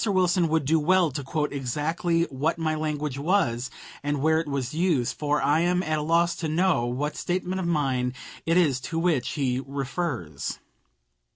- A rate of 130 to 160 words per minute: No, average, 180 wpm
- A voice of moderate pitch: Yes, medium, 155 Hz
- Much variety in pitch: No, average, 3.7 semitones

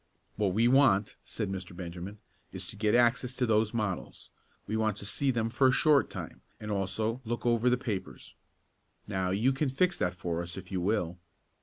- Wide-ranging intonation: No, average, 4.3 semitones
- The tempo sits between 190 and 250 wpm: Yes, average, 195 wpm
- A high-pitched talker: No, low, 110 Hz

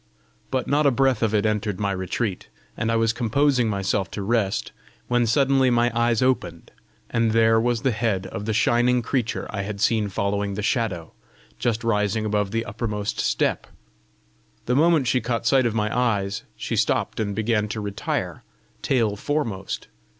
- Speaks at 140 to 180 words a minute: Yes, average, 170 wpm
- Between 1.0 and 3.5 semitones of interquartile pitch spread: Yes, average, 2.9 semitones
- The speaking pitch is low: Yes, low, 115 Hz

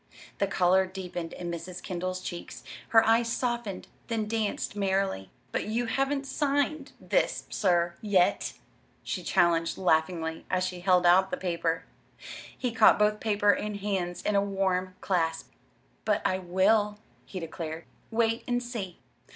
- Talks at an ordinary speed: Yes, average, 145 wpm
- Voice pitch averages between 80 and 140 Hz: No, high, 190 Hz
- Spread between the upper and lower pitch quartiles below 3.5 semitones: No, average, 3.8 semitones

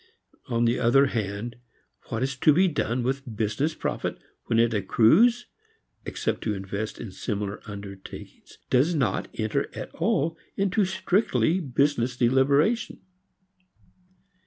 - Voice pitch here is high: No, low, 125 Hz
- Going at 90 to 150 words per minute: Yes, slow, 135 wpm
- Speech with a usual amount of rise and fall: No, wide, 5.8 semitones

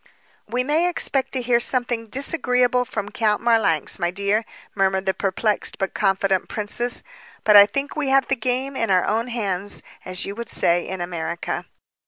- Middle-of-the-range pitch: No, high, 220 Hz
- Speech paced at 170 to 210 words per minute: Yes, average, 175 wpm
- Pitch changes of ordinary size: Yes, average, 4.4 semitones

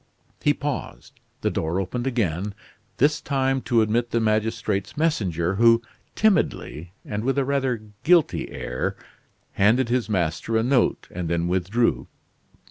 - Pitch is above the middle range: No, low, 115 Hz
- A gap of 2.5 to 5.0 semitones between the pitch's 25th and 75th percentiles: No, wide, 5.6 semitones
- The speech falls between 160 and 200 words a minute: No, slow, 135 wpm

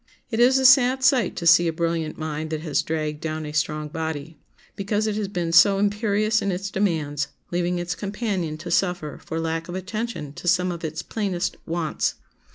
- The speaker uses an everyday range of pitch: Yes, average, 4.3 semitones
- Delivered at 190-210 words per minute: Yes, average, 195 wpm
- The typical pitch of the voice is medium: Yes, medium, 175 Hz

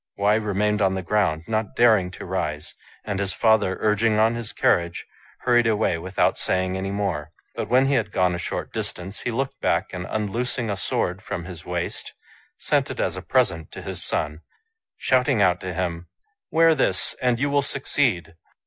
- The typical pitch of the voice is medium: No, low, 105 Hz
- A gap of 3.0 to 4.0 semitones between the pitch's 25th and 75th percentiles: No, average, 4.5 semitones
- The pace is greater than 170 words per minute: Yes, average, 195 wpm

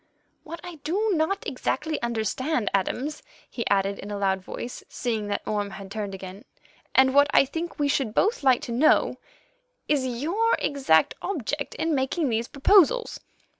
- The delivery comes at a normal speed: Yes, average, 165 wpm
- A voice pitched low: No, very high, 265 Hz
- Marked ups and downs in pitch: Yes, wide, 7.0 semitones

